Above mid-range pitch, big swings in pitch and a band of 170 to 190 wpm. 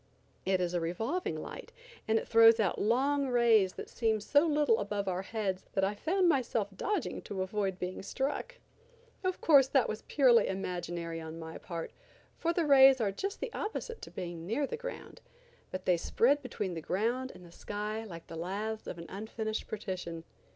Yes: high, 215 Hz; wide, 6.4 semitones; average, 185 wpm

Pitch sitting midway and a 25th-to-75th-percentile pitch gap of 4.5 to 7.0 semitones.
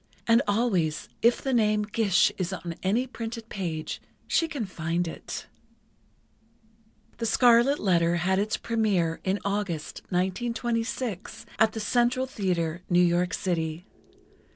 No: high, 200 Hz; average, 4.9 semitones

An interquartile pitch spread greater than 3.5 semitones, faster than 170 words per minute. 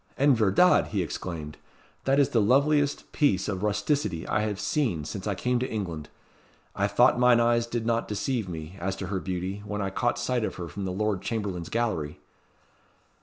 Yes: average, 4.3 semitones; average, 190 wpm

